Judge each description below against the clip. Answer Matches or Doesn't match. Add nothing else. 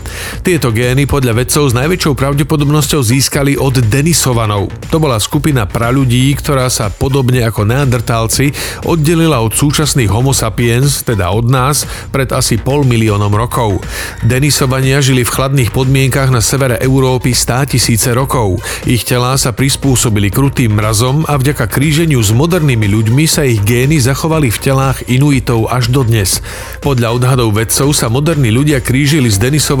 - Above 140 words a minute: Matches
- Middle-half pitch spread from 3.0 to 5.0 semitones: Matches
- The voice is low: Matches